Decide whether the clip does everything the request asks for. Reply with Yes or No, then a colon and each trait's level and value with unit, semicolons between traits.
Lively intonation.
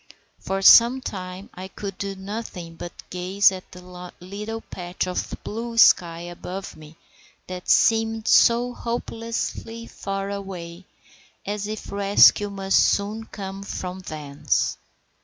No: average, 3.1 semitones